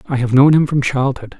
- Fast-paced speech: Yes, fast, 260 wpm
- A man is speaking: Yes, male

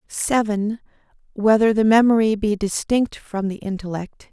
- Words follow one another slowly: Yes, slow, 125 wpm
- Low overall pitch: No, high, 210 Hz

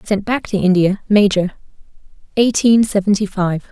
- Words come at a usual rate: No, slow, 130 wpm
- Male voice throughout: No, female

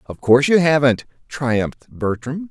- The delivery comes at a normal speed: Yes, average, 145 wpm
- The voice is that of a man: Yes, male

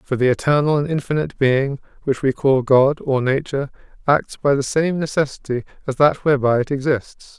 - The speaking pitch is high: No, medium, 140 Hz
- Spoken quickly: No, average, 180 wpm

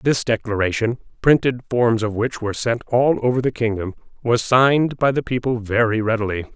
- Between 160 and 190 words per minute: Yes, average, 175 wpm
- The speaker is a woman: No, male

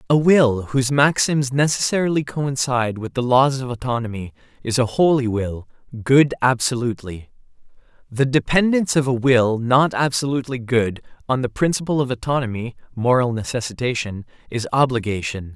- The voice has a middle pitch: No, low, 125 Hz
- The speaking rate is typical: No, slow, 130 wpm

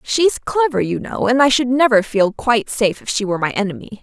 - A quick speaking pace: Yes, fast, 240 wpm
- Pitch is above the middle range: Yes, high, 235 Hz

